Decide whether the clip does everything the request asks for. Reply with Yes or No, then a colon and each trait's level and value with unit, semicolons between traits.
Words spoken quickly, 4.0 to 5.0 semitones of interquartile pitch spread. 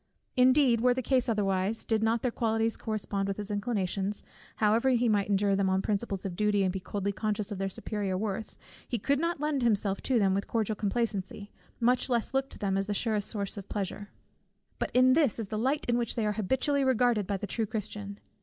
No: fast, 215 wpm; average, 3.2 semitones